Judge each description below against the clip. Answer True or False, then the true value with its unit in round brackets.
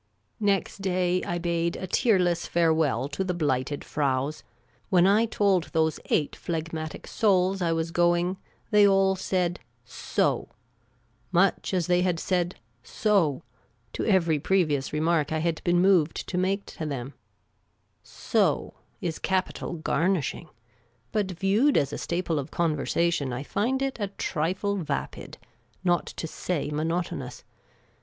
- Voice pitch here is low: False (175 Hz)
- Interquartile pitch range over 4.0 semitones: False (3.5 semitones)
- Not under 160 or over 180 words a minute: False (150 wpm)